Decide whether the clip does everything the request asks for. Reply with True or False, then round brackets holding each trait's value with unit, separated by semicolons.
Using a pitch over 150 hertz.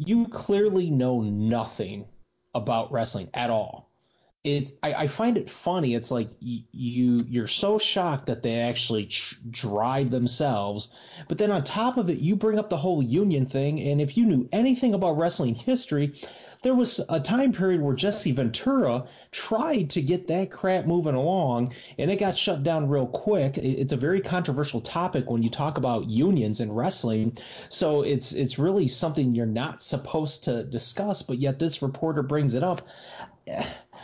False (145 Hz)